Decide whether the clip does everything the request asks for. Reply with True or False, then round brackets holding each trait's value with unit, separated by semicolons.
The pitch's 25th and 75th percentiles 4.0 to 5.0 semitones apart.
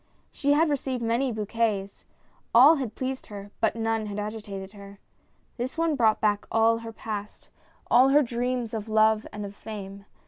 False (3.2 semitones)